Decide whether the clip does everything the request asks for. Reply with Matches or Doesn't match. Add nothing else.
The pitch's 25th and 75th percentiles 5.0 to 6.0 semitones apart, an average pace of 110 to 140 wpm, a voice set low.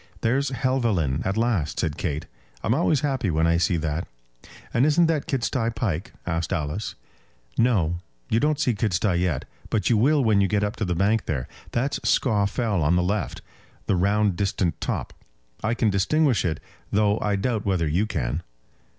Doesn't match